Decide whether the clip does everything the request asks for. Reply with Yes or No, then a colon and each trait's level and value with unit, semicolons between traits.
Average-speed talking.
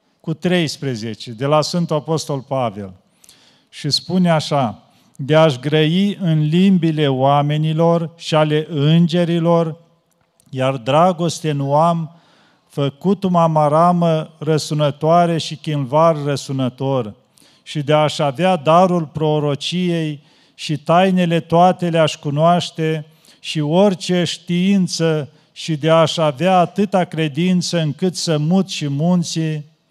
No: slow, 110 wpm